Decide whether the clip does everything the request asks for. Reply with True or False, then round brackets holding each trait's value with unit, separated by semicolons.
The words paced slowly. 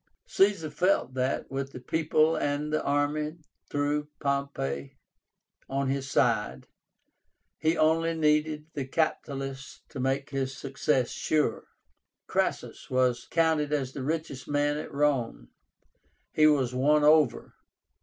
True (125 wpm)